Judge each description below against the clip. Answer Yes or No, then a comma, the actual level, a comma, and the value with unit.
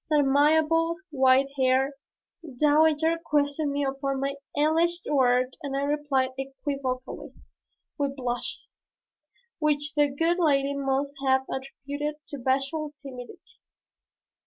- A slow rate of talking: Yes, slow, 110 wpm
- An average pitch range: No, narrow, 2.0 semitones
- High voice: Yes, very high, 280 Hz